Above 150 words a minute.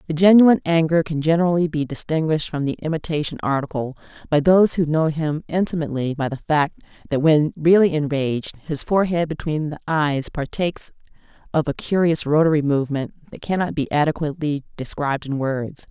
Yes: average, 160 wpm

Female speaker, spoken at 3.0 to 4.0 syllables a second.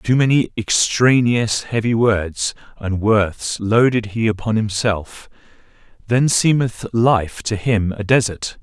No: male; 3.7 syllables/s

